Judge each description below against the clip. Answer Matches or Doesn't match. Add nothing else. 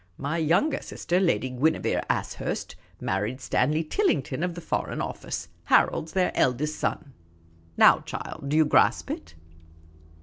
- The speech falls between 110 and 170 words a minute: Matches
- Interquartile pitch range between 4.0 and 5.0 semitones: Matches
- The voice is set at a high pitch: Doesn't match